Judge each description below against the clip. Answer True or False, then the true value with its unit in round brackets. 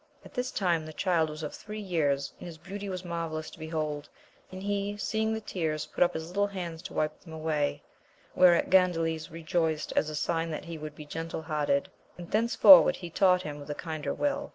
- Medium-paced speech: False (210 wpm)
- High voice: False (165 Hz)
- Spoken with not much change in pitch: False (3.2 semitones)